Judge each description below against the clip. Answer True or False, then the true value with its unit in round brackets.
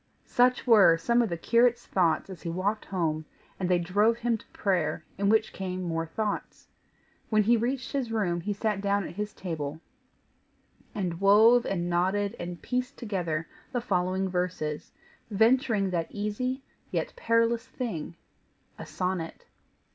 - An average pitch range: True (4.7 semitones)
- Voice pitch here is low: False (200 Hz)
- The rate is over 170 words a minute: False (155 wpm)